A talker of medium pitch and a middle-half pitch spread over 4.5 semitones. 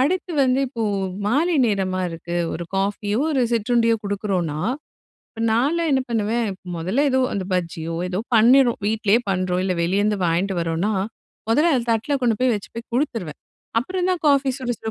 No: high, 220 Hz; wide, 5.5 semitones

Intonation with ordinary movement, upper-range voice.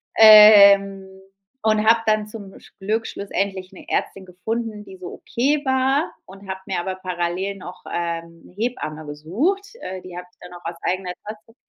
Yes: average, 3.4 semitones; high, 195 Hz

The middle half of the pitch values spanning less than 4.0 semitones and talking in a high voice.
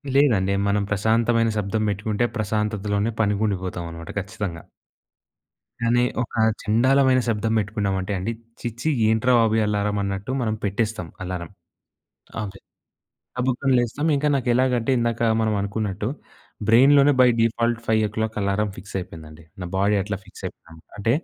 No: average, 2.9 semitones; low, 105 Hz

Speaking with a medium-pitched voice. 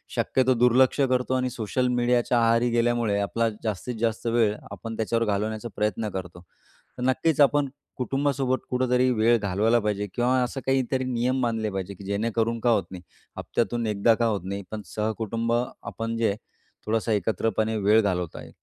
No: low, 115 Hz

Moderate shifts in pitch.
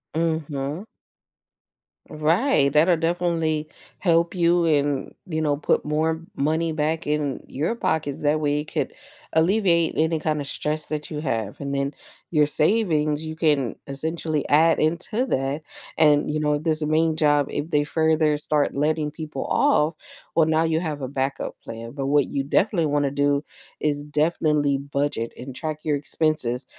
No: narrow, 1.9 semitones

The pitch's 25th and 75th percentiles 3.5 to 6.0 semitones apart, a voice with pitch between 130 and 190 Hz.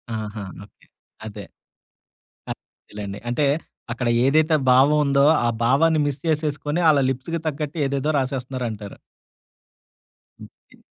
Yes: average, 3.9 semitones; low, 135 Hz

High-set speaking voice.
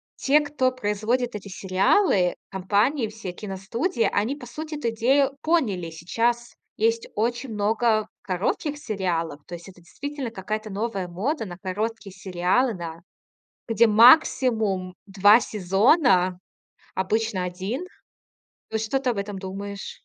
Yes: high, 215 Hz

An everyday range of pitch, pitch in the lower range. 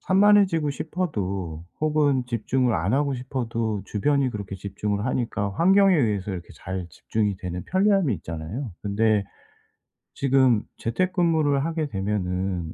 No: wide, 7.2 semitones; low, 115 Hz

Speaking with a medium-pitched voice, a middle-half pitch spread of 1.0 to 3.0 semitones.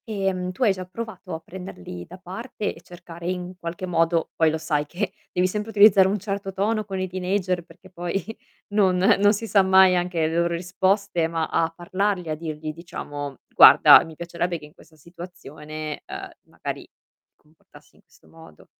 Yes: medium, 180 Hz; average, 2.7 semitones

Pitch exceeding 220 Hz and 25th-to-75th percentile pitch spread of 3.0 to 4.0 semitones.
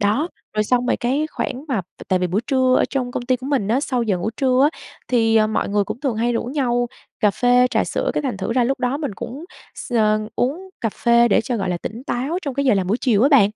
Yes: high, 245 Hz; average, 3.7 semitones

